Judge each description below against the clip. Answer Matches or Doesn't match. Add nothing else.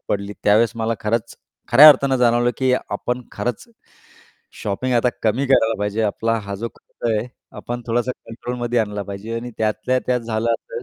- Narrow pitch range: Matches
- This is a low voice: Matches